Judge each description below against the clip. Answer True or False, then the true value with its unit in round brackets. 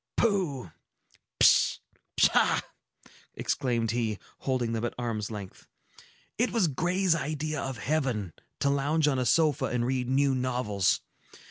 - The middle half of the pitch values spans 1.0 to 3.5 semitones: False (4.6 semitones)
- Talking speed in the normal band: False (130 wpm)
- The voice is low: True (130 Hz)